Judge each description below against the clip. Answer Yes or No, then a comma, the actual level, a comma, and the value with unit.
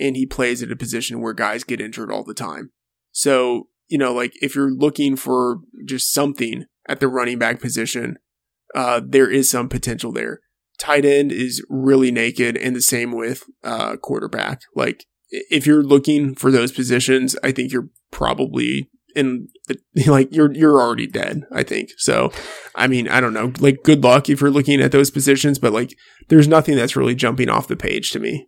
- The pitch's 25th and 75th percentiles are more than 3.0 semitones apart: No, narrow, 2.6 semitones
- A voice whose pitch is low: Yes, low, 130 Hz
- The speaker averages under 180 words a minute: No, average, 195 wpm